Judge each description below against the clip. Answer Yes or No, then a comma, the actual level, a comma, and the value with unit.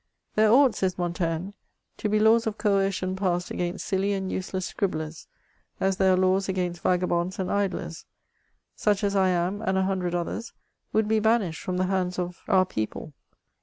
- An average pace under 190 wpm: Yes, average, 175 wpm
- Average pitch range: No, narrow, 2.1 semitones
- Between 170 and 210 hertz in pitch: Yes, high, 190 Hz